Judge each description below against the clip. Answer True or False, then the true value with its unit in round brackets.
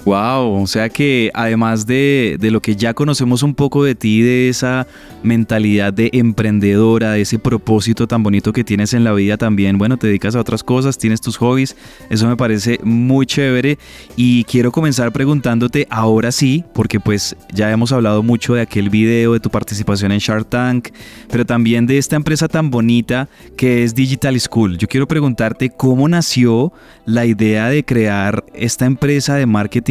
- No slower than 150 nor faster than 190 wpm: True (180 wpm)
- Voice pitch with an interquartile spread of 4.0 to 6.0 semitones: False (2.8 semitones)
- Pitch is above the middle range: False (120 Hz)